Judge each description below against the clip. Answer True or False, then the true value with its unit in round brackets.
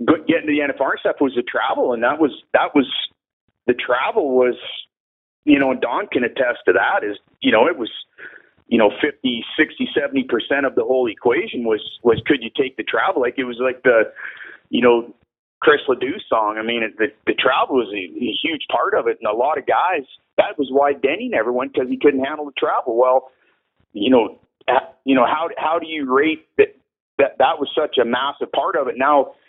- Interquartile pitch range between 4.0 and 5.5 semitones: True (4.5 semitones)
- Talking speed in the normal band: False (220 wpm)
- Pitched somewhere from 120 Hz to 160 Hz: True (140 Hz)